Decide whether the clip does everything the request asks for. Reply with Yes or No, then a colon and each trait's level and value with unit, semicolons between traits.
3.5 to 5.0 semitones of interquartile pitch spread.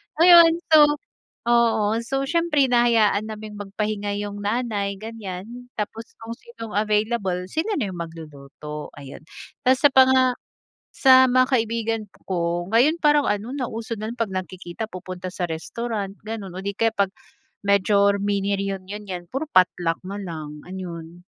Yes: average, 4.1 semitones